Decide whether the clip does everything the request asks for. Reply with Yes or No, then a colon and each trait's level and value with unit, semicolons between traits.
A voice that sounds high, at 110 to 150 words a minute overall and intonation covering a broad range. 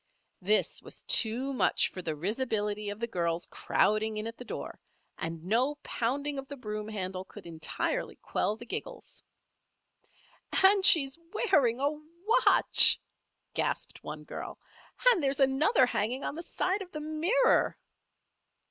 Yes: high, 245 Hz; average, 145 wpm; wide, 6.0 semitones